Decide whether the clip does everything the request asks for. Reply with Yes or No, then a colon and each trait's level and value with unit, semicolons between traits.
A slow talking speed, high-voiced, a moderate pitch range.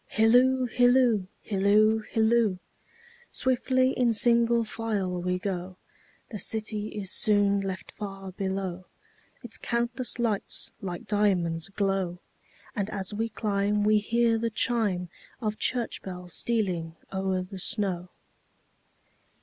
Yes: slow, 100 wpm; high, 210 Hz; average, 3.5 semitones